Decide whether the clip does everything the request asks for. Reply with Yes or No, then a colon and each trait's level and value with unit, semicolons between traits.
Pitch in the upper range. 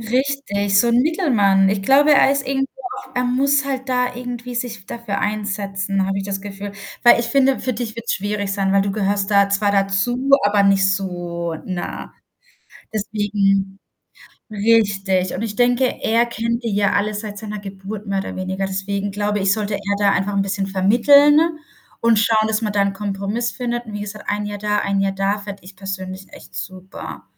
Yes: high, 205 Hz